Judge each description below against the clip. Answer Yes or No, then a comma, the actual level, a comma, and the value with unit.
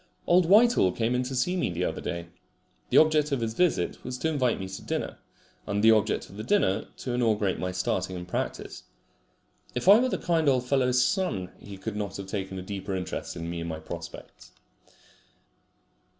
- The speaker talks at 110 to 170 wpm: No, average, 195 wpm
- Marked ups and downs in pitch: Yes, wide, 7.1 semitones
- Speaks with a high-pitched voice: No, low, 110 Hz